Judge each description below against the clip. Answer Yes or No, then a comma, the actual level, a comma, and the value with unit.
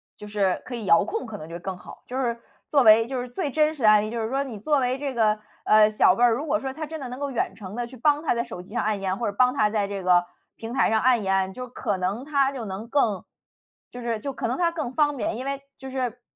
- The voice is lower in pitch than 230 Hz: No, high, 235 Hz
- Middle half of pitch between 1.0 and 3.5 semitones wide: No, average, 4.2 semitones